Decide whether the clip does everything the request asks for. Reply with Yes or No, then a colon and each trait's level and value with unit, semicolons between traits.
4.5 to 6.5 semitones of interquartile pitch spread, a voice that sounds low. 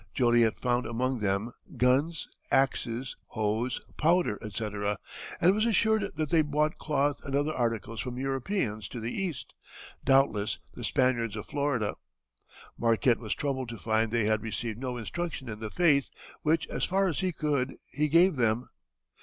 Yes: average, 5.1 semitones; low, 125 Hz